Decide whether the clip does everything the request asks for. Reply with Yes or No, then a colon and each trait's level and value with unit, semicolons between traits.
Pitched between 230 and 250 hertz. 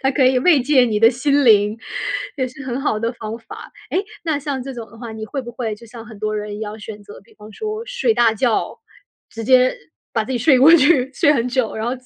Yes: high, 245 Hz